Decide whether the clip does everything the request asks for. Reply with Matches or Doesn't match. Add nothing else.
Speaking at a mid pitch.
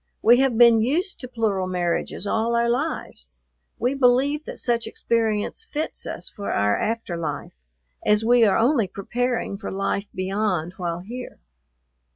Doesn't match